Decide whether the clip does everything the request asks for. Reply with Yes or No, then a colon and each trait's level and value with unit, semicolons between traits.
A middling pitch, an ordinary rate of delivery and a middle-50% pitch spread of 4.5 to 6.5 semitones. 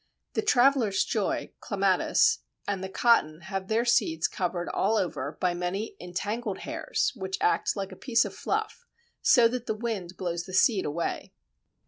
No: high, 200 Hz; average, 160 wpm; average, 4.9 semitones